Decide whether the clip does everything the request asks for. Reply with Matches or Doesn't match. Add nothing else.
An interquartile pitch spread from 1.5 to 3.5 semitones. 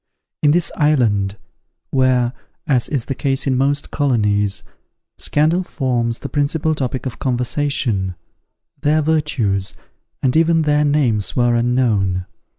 Doesn't match